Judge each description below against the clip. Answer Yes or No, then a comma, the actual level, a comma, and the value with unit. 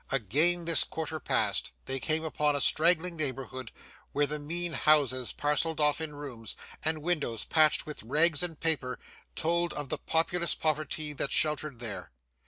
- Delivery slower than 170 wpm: Yes, average, 160 wpm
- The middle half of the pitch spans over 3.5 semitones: No, average, 2.7 semitones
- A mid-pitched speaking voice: Yes, medium, 150 Hz